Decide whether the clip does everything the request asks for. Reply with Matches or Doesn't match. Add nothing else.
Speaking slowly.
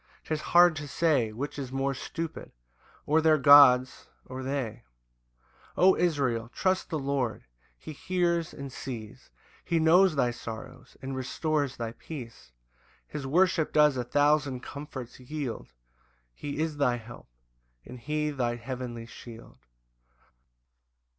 Matches